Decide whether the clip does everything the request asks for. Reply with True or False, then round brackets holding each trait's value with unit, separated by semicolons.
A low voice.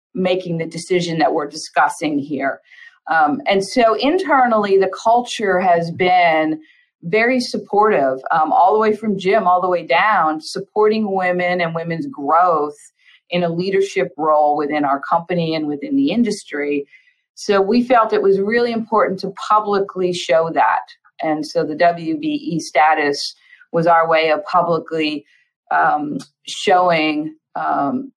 False (180 Hz)